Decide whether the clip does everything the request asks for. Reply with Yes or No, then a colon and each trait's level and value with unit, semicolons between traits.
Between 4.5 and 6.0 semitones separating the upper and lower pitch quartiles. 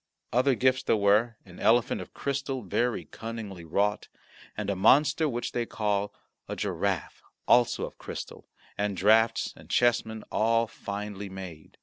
No: average, 3.1 semitones